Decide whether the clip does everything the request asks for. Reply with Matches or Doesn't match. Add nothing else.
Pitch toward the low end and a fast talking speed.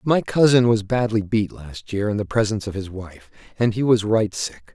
Matches